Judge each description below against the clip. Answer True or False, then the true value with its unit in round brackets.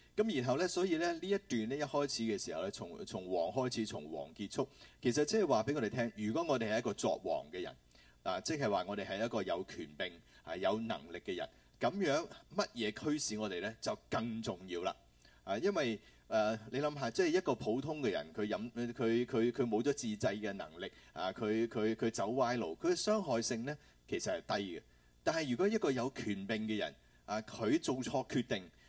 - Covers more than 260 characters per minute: True (295 characters per minute)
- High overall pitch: False (120 Hz)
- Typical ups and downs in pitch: False (5.8 semitones)